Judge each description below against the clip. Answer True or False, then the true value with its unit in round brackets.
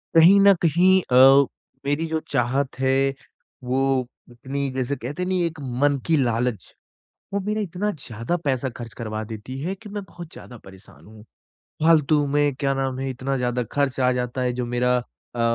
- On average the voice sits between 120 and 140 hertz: True (135 Hz)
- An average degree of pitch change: True (4.5 semitones)